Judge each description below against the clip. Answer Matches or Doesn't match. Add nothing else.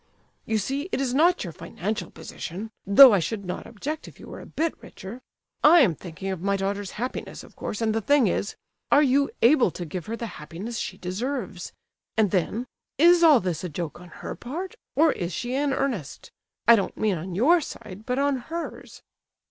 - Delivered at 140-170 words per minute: Doesn't match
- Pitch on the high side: Matches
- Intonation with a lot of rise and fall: Matches